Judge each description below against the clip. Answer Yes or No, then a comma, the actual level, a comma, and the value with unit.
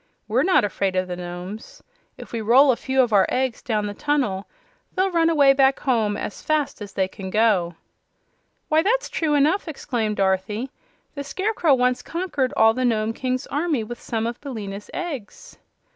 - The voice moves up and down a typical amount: No, wide, 5.8 semitones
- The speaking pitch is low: No, high, 245 Hz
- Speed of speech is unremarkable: Yes, average, 180 wpm